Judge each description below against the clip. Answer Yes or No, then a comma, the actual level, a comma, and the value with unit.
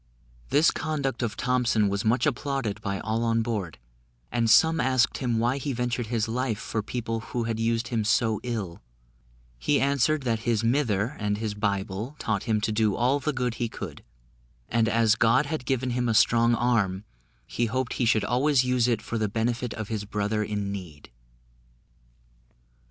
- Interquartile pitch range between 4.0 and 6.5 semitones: No, average, 2.7 semitones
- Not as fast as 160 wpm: No, average, 180 wpm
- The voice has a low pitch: Yes, low, 115 Hz